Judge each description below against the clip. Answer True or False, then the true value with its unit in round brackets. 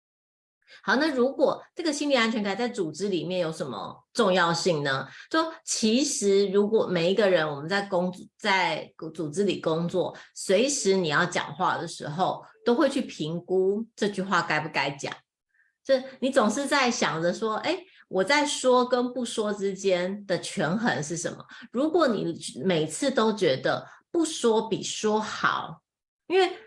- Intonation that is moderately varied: False (6.7 semitones)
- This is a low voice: False (205 Hz)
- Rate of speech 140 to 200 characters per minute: False (225 characters per minute)